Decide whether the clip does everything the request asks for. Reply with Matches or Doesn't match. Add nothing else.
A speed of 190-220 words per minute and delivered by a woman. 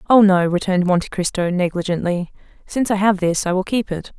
Matches